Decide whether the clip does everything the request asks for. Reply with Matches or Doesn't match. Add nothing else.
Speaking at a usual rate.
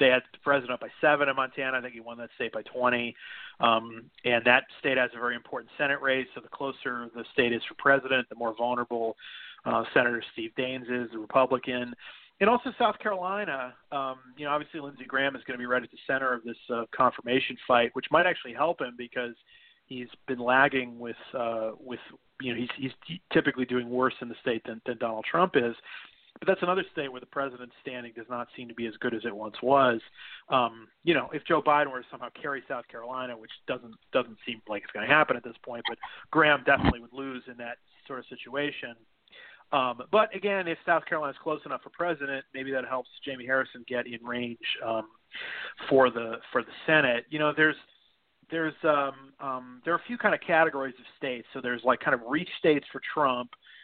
Doesn't match